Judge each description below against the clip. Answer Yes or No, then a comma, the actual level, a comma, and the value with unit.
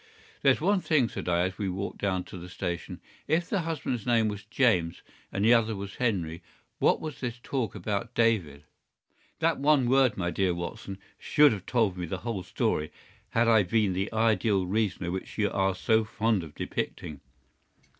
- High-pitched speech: No, low, 105 Hz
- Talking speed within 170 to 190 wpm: Yes, average, 185 wpm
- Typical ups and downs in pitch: Yes, average, 4.2 semitones